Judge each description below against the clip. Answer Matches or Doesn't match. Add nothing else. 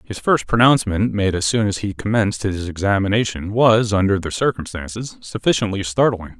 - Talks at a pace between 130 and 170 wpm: Matches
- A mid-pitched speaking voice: Doesn't match